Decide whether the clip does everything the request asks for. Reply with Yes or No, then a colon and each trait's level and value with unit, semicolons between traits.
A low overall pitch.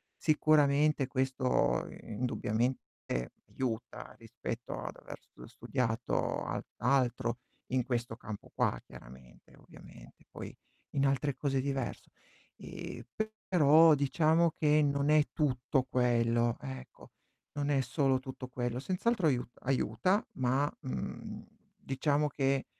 Yes: low, 130 Hz